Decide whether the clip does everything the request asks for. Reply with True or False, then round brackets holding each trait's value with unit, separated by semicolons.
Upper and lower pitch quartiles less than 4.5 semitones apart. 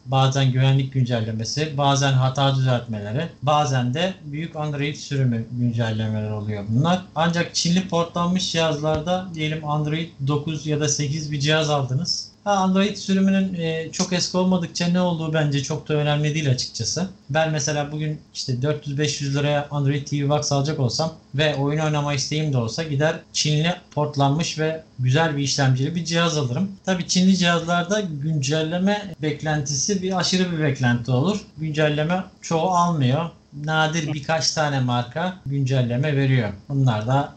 True (3.4 semitones)